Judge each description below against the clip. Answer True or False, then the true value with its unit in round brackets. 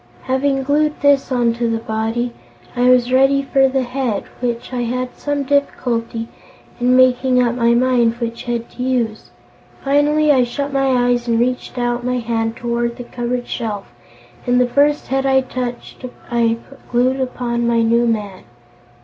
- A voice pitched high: True (245 Hz)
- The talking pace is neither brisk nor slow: True (165 wpm)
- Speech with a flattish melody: True (1.9 semitones)